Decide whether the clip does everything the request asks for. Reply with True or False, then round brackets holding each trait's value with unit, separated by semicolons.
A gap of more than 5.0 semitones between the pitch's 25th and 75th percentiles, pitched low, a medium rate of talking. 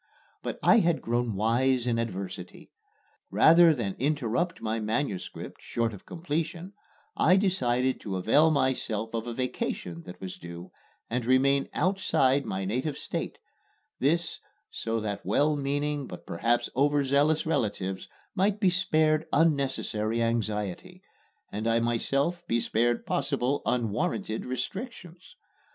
False (5.5 semitones; 130 Hz; 125 wpm)